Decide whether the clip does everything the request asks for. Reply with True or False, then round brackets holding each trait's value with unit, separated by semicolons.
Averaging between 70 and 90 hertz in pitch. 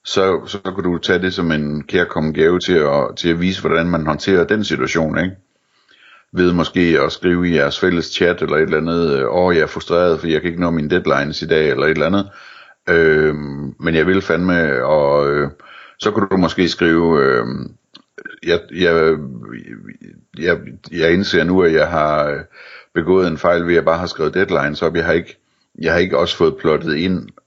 True (85 Hz)